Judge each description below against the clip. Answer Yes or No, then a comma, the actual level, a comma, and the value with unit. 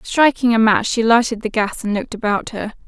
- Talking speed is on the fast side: Yes, fast, 230 wpm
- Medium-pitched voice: No, high, 225 Hz